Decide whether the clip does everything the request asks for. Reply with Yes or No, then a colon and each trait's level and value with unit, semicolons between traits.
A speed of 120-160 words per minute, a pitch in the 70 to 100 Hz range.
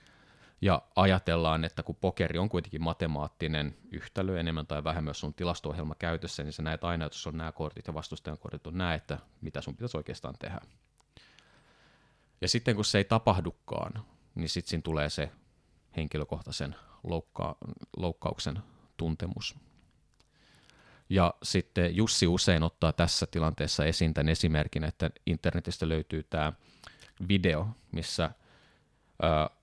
Yes: average, 140 wpm; very low, 80 Hz